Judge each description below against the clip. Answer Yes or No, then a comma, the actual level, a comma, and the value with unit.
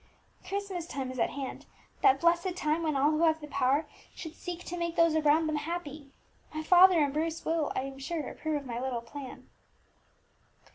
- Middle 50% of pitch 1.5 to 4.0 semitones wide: Yes, average, 3.3 semitones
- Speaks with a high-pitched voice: Yes, very high, 310 Hz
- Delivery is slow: No, average, 195 wpm